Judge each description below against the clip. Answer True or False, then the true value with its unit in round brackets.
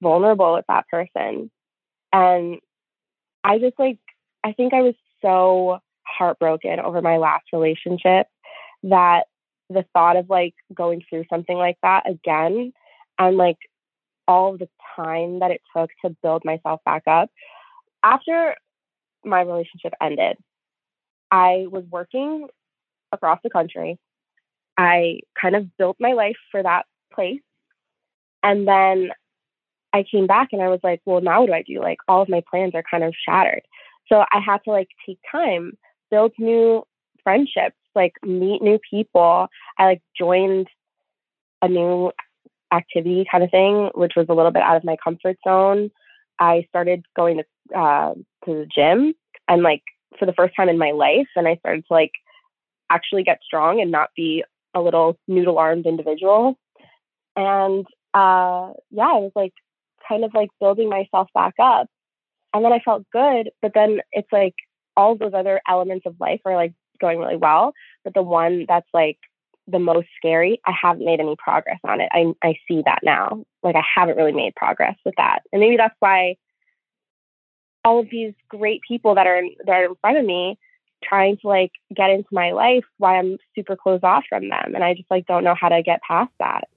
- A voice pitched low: False (185 Hz)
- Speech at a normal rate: True (175 wpm)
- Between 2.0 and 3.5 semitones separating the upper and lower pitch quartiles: True (3.1 semitones)